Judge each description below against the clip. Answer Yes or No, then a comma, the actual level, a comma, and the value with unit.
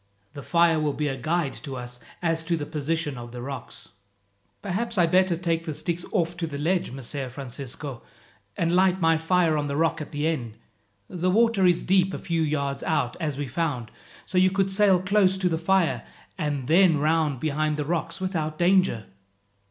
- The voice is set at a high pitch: No, medium, 165 Hz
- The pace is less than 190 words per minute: No, average, 200 wpm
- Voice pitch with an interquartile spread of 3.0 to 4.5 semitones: Yes, average, 3.8 semitones